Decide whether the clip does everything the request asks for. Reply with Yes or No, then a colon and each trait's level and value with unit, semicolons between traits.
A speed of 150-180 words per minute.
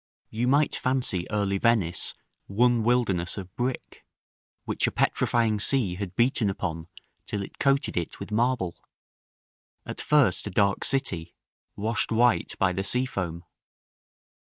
No: slow, 135 wpm